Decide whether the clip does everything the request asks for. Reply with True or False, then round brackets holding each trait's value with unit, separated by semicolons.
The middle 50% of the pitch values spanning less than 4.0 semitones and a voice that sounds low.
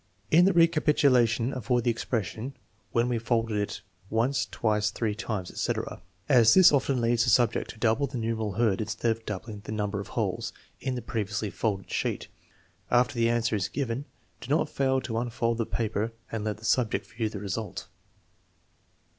True (2.4 semitones; 115 Hz)